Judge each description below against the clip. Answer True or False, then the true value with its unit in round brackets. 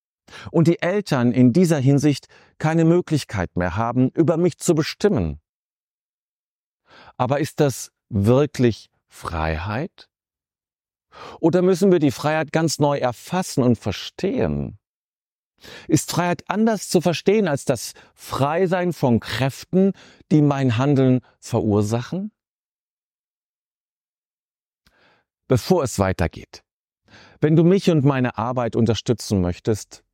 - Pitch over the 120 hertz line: True (140 Hz)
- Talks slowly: True (110 wpm)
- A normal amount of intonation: False (6.6 semitones)